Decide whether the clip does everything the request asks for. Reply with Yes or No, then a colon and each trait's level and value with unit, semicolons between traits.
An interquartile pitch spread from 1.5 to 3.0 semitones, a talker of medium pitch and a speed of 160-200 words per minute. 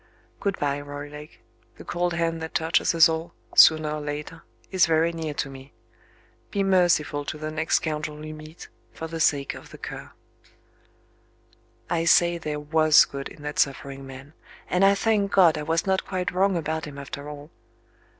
Yes: narrow, 2.4 semitones; medium, 155 Hz; average, 180 wpm